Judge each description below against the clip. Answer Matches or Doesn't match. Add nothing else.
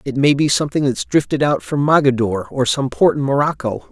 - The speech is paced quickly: Matches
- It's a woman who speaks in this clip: Doesn't match